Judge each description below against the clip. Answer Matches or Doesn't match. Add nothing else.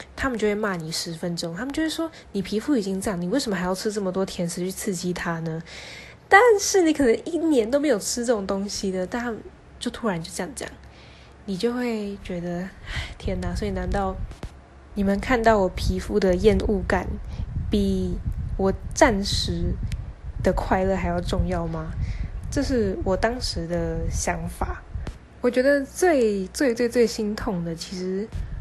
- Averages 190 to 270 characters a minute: Matches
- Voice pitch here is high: Matches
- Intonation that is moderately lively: Doesn't match